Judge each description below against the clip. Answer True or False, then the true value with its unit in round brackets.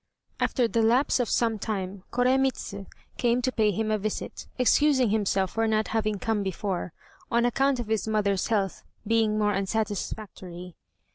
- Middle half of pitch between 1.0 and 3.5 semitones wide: True (2.8 semitones)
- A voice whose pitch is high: True (220 Hz)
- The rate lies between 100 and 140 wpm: False (155 wpm)